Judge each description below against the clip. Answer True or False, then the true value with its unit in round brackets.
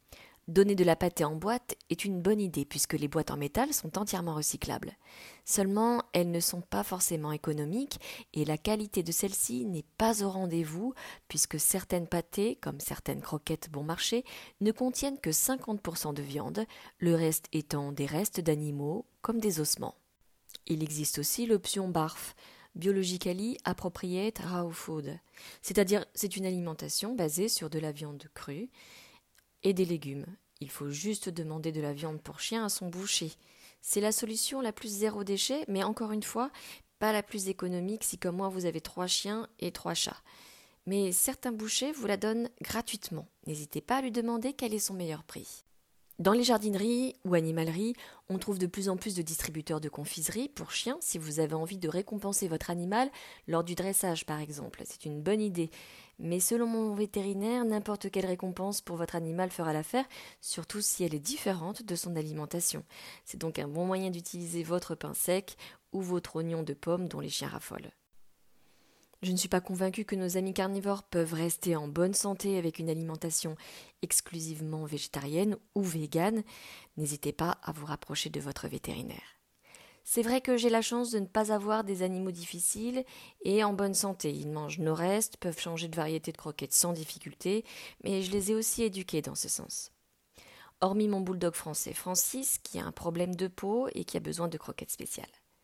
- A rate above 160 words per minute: True (180 wpm)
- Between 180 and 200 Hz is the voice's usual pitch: True (185 Hz)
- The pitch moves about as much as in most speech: True (4.5 semitones)